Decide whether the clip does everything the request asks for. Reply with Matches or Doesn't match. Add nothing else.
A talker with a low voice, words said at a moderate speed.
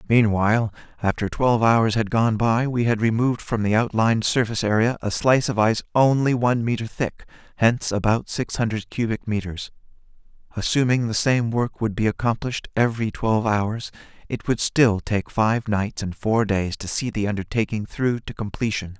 Matches